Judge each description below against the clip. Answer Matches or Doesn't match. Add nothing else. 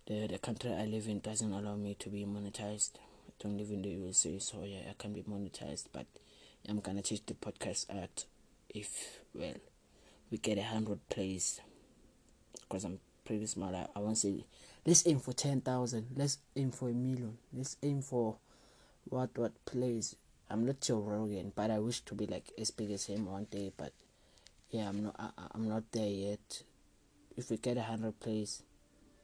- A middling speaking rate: Matches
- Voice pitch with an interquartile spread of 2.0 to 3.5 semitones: Matches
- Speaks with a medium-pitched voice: Doesn't match